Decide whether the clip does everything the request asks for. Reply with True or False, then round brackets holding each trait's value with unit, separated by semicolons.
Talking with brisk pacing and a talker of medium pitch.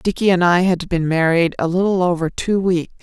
True (220 wpm; 175 Hz)